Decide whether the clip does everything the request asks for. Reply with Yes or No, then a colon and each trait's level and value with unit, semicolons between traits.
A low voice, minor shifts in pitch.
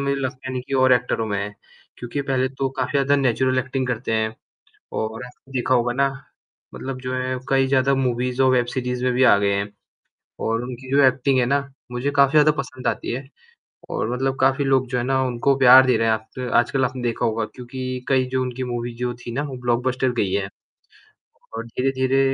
Yes: low, 130 Hz; narrow, 1.6 semitones